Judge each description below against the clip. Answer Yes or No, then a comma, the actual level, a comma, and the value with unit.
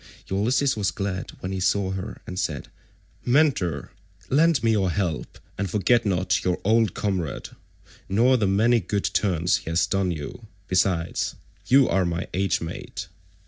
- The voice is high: No, very low, 95 Hz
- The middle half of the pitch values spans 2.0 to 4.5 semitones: Yes, average, 3.6 semitones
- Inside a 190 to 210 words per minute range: No, average, 155 wpm